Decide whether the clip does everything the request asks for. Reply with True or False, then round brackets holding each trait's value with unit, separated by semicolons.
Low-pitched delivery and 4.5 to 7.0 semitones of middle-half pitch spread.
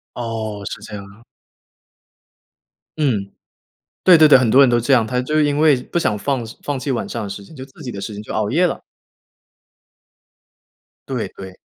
True (120 Hz; 5.2 semitones)